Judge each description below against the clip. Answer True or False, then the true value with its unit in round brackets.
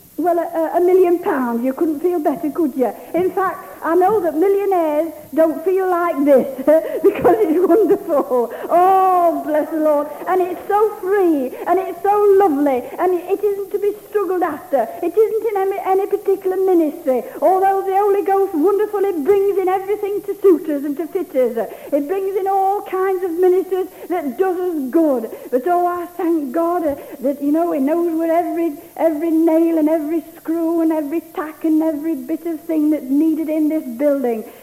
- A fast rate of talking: False (185 wpm)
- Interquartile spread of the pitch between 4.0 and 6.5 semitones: False (3.5 semitones)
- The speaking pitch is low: False (340 Hz)